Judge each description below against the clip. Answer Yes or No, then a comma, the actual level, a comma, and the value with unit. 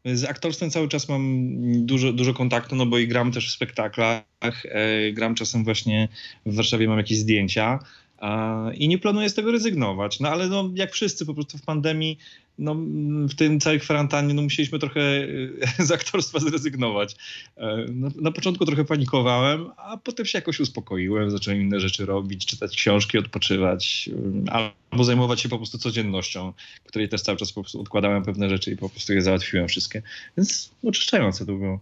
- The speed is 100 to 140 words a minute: No, fast, 170 wpm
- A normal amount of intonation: No, wide, 6.2 semitones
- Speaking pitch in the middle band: No, low, 120 Hz